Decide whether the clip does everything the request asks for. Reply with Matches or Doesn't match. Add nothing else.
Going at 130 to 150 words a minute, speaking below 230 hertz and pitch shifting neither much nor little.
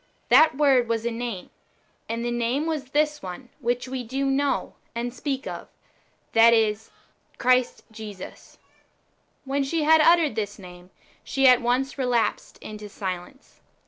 Doesn't match